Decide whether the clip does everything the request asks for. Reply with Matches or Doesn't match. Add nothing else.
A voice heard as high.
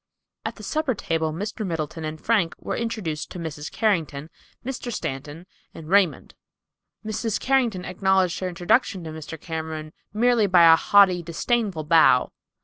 Doesn't match